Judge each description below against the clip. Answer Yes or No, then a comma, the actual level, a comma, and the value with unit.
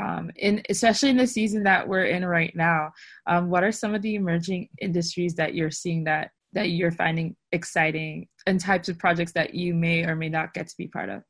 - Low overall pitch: No, medium, 175 Hz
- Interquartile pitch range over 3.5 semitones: No, average, 2.8 semitones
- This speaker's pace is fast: Yes, fast, 225 wpm